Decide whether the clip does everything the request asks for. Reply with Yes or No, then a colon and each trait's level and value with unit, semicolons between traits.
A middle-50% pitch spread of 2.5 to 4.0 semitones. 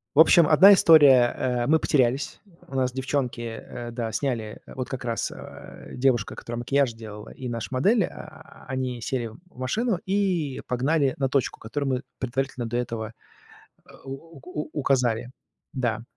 Yes: average, 3.0 semitones